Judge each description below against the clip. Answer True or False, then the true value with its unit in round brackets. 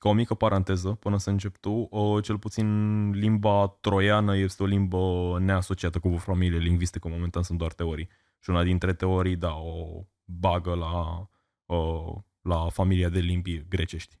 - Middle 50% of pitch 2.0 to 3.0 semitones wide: True (2.5 semitones)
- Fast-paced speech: False (155 wpm)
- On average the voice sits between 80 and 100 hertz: True (95 Hz)